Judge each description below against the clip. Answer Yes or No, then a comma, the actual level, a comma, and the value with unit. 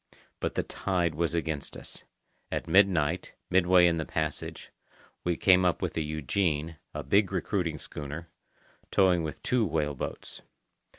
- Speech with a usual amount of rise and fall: Yes, average, 3.1 semitones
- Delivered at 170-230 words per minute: No, average, 145 wpm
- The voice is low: Yes, very low, 85 Hz